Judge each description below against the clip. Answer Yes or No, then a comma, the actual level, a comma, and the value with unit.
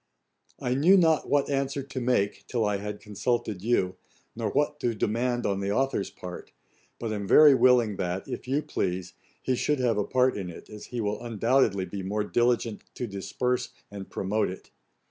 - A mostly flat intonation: No, average, 4.2 semitones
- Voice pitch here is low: Yes, low, 115 Hz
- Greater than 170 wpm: Yes, average, 185 wpm